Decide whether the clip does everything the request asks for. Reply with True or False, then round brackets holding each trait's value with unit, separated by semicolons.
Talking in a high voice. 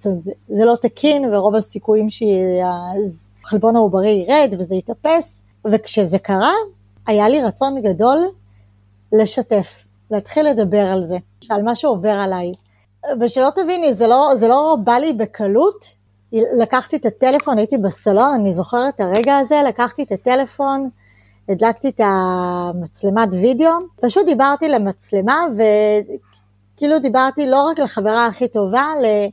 True (220 Hz)